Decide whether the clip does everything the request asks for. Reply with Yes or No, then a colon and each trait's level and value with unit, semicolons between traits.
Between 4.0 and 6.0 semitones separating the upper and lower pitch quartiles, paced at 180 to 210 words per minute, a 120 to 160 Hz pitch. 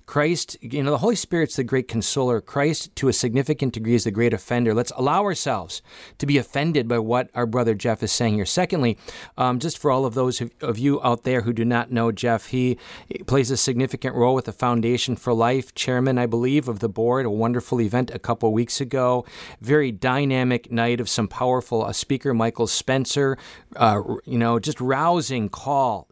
No: narrow, 2.5 semitones; fast, 205 wpm; low, 125 Hz